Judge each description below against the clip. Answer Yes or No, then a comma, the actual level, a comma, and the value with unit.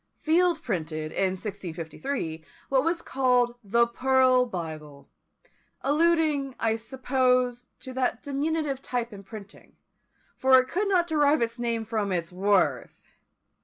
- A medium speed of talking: No, slow, 130 wpm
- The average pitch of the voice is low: No, very high, 250 Hz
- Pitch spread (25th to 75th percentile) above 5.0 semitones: Yes, wide, 5.6 semitones